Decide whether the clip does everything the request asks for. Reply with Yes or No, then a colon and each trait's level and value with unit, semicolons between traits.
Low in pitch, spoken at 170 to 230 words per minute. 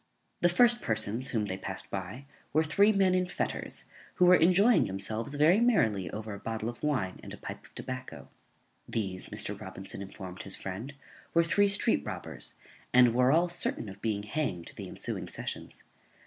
Yes: low, 120 Hz; average, 180 wpm